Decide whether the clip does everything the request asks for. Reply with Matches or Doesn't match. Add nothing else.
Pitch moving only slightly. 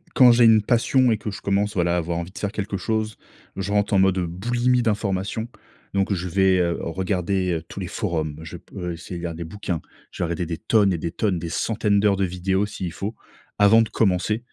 Doesn't match